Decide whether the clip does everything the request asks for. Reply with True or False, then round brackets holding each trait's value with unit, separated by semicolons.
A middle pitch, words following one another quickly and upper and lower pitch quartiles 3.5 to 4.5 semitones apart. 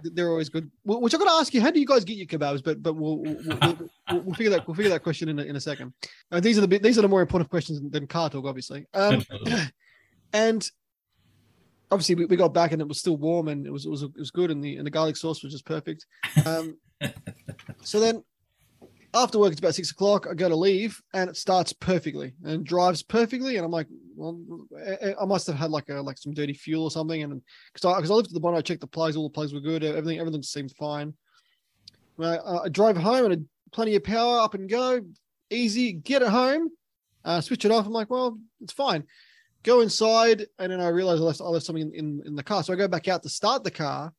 False (175 Hz; 250 wpm; 5.4 semitones)